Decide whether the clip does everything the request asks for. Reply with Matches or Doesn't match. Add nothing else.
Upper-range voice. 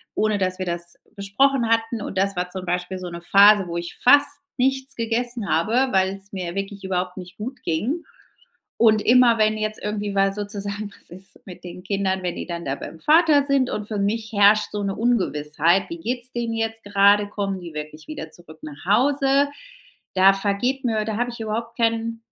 Matches